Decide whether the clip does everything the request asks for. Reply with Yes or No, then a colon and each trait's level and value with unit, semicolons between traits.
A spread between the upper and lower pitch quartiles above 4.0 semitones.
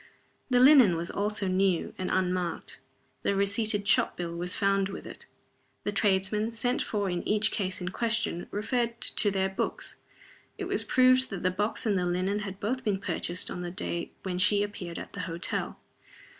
No: narrow, 2.6 semitones